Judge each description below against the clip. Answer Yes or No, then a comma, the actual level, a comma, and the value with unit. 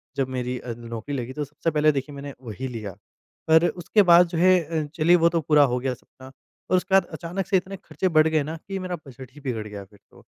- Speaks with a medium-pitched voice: Yes, medium, 150 Hz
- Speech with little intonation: No, average, 5.2 semitones